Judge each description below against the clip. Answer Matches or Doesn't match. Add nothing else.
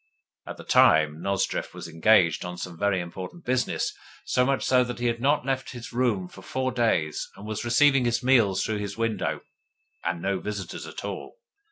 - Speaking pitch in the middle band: Doesn't match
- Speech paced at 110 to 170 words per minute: Doesn't match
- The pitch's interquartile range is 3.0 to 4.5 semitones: Doesn't match